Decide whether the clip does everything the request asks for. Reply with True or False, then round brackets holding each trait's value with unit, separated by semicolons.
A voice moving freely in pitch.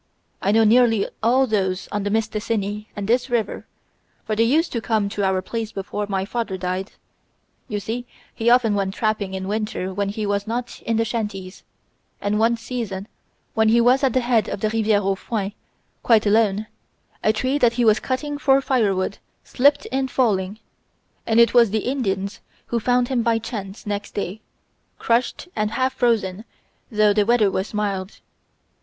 False (2.8 semitones)